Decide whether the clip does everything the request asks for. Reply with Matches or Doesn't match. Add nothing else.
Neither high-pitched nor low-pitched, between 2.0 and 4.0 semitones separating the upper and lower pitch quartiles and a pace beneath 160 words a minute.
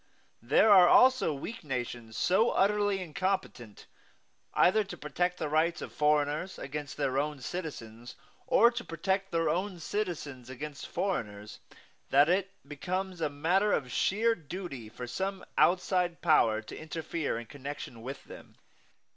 Doesn't match